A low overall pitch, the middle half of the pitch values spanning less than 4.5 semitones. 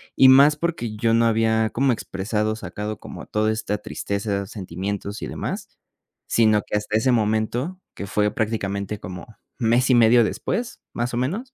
Yes: low, 110 Hz; narrow, 2.5 semitones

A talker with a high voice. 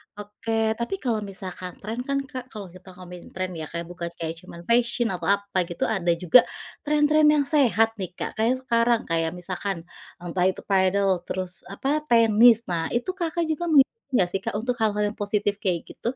Yes: high, 210 Hz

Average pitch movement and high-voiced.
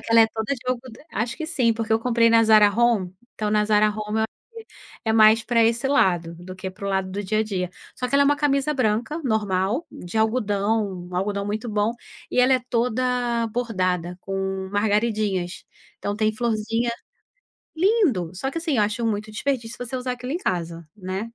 Yes: average, 3.4 semitones; high, 220 Hz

